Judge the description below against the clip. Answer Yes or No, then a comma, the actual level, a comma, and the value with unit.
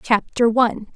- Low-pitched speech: No, high, 230 Hz